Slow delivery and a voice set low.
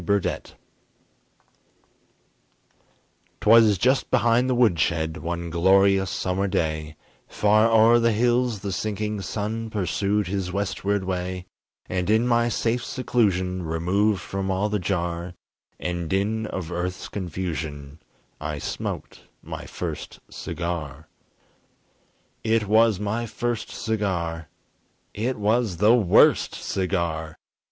Yes: slow, 110 wpm; very low, 95 Hz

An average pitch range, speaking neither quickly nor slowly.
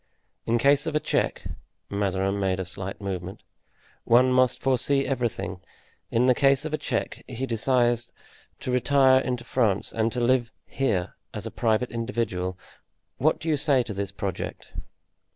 Yes: average, 4.7 semitones; average, 160 wpm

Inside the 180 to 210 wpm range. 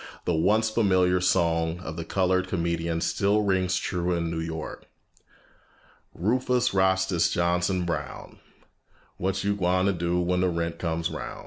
No: average, 145 wpm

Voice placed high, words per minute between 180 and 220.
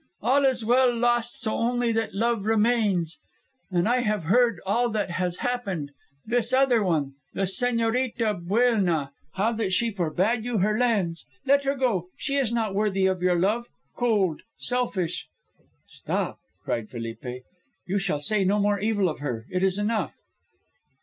No: high, 215 Hz; average, 165 wpm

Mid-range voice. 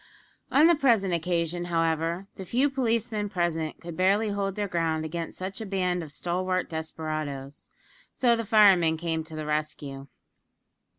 Yes: medium, 175 Hz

